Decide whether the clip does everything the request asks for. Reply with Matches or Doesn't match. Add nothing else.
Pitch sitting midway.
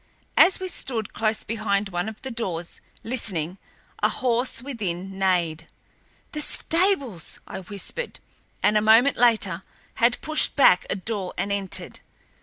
Doesn't match